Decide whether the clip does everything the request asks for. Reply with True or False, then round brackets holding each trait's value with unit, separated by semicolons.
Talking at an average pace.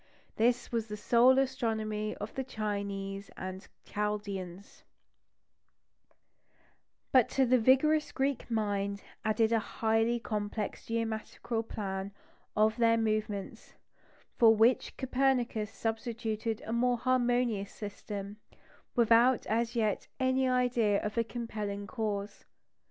False (115 wpm)